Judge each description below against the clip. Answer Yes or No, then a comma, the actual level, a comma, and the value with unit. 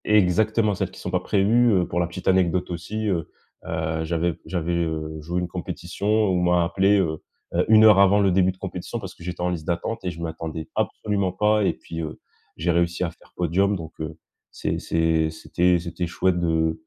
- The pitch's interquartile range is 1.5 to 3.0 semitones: Yes, average, 2.7 semitones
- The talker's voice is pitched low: Yes, very low, 90 Hz